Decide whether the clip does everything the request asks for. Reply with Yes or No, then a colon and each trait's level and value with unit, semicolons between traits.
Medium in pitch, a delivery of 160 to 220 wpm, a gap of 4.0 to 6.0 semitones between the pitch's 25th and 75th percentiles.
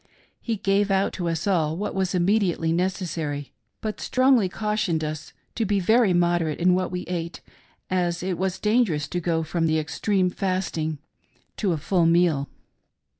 No: medium, 180 Hz; average, 175 wpm; average, 3.2 semitones